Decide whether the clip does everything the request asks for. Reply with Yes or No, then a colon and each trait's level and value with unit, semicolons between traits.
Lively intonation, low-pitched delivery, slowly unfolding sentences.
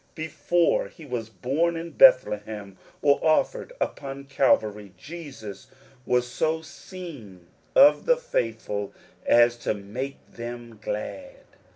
Yes: wide, 7.1 semitones; low, 130 Hz; slow, 110 wpm